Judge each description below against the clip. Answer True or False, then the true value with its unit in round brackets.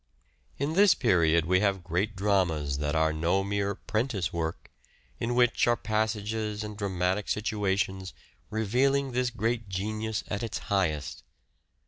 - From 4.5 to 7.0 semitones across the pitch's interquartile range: False (3.4 semitones)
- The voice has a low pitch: True (100 Hz)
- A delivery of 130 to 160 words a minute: True (140 wpm)